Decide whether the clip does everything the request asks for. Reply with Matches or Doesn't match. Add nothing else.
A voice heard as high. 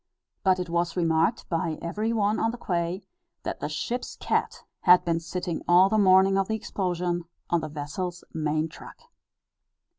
Doesn't match